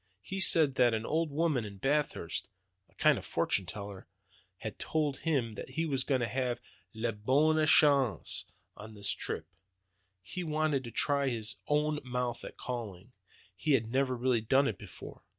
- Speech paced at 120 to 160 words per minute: No, average, 170 wpm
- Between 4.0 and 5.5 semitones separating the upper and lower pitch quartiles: Yes, average, 5.1 semitones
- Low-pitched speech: Yes, low, 130 Hz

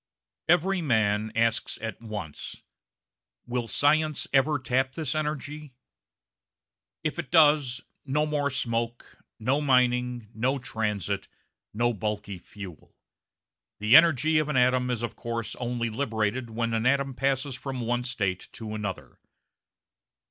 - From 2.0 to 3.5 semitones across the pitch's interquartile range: No, average, 4.1 semitones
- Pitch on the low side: Yes, low, 125 Hz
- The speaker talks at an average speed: No, slow, 125 wpm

